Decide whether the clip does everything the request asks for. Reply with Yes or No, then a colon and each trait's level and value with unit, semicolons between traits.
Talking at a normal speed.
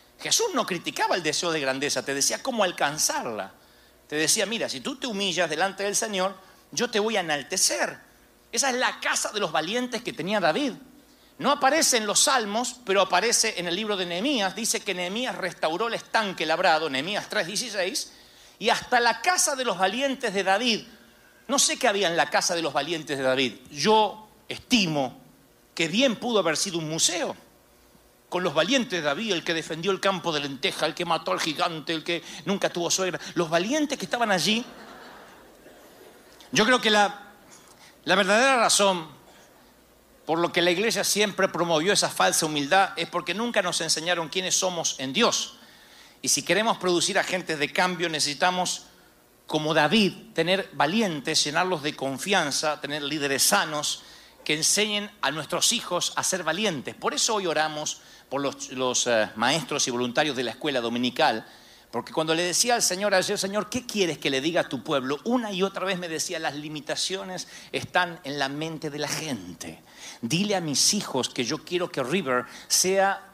Yes: average, 180 wpm